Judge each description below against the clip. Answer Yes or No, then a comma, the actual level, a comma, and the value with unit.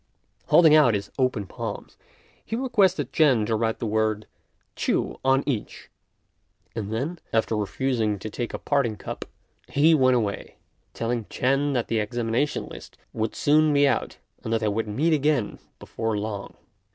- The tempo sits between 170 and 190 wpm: No, average, 160 wpm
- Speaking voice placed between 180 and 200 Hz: No, low, 120 Hz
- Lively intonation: No, average, 4.7 semitones